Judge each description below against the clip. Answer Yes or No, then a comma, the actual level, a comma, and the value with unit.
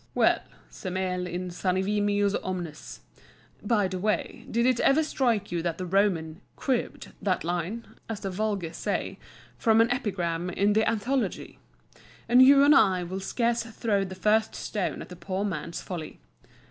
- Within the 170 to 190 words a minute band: No, average, 155 wpm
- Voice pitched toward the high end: Yes, high, 200 Hz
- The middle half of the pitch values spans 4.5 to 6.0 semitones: No, average, 3.8 semitones